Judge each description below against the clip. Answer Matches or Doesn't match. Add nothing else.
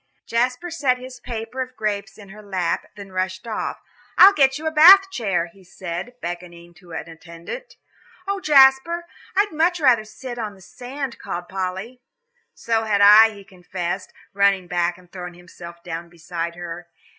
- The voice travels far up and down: Matches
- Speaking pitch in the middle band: Doesn't match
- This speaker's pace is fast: Doesn't match